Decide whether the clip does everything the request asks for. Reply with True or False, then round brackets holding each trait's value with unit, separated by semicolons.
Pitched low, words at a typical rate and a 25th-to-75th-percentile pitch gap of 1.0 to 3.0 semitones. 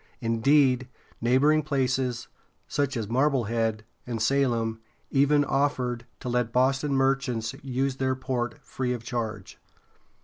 False (125 Hz; 130 wpm; 2.6 semitones)